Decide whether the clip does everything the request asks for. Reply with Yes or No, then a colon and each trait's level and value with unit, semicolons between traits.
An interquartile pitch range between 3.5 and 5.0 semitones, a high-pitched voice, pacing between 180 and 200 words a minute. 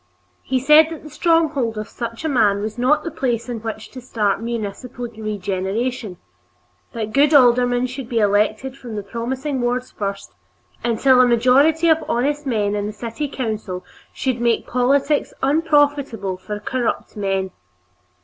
No: average, 4.0 semitones; high, 240 Hz; average, 155 wpm